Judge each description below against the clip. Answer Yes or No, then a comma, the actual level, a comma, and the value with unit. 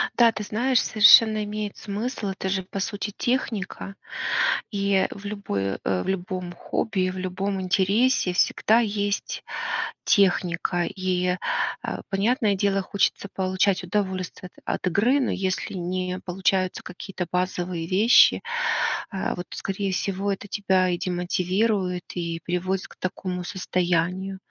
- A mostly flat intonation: Yes, narrow, 1.9 semitones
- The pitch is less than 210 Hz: Yes, high, 190 Hz